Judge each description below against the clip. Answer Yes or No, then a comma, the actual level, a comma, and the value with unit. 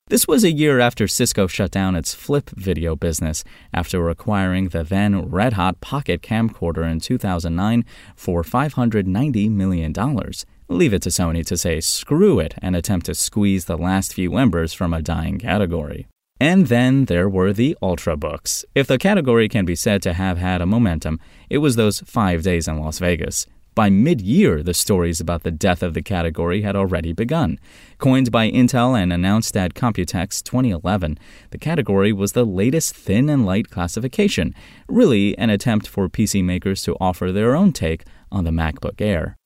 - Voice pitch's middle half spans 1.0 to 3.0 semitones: No, average, 5.0 semitones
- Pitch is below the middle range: Yes, very low, 95 Hz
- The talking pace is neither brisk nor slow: Yes, average, 175 wpm